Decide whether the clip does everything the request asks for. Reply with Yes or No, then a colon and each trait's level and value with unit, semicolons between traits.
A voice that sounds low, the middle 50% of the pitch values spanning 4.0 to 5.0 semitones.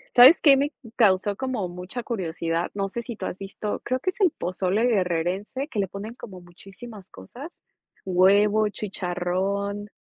No: high, 200 Hz; average, 4.4 semitones